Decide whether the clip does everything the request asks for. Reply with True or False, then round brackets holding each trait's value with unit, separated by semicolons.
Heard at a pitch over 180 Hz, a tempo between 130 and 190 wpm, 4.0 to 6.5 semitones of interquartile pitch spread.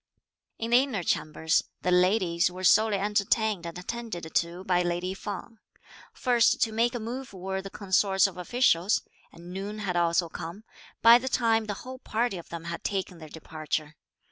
True (190 Hz; 175 wpm; 4.4 semitones)